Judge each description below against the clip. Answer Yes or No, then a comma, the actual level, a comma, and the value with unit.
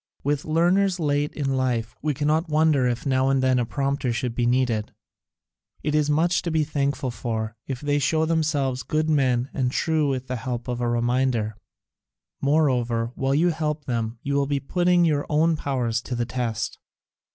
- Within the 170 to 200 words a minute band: Yes, average, 185 wpm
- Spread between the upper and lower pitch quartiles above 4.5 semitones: No, average, 3.8 semitones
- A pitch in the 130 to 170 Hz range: Yes, low, 135 Hz